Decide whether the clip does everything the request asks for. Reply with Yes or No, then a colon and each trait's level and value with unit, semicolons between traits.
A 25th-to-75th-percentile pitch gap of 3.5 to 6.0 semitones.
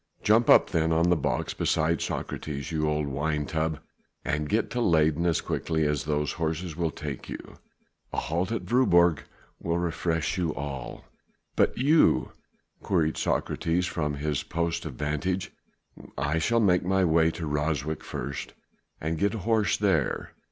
No: average, 2.8 semitones